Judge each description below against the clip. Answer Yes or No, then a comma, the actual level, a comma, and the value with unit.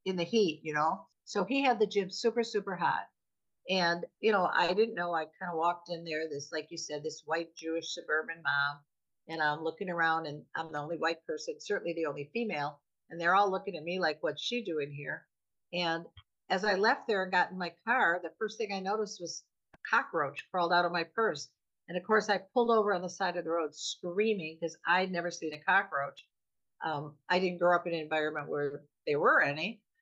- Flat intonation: No, average, 3.8 semitones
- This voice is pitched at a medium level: Yes, medium, 170 Hz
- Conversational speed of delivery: No, fast, 225 wpm